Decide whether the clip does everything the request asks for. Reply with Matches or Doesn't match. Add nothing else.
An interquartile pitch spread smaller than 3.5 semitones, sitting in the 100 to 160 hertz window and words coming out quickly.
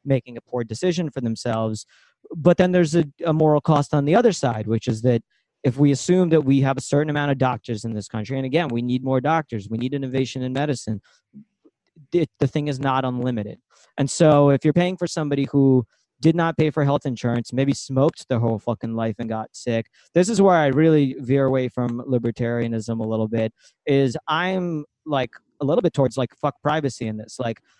Doesn't match